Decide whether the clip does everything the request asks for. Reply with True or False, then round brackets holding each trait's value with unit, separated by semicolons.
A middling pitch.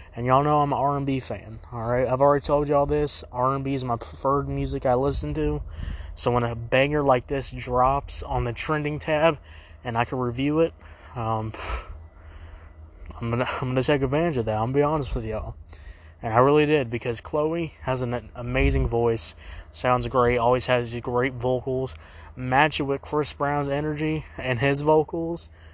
False (125 Hz)